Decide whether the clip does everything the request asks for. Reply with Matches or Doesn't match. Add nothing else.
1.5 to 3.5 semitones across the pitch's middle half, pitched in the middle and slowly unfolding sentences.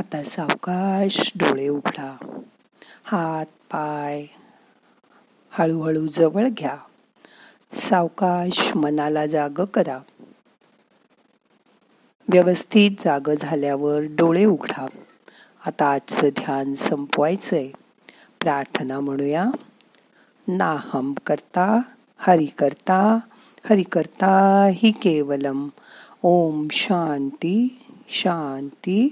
Doesn't match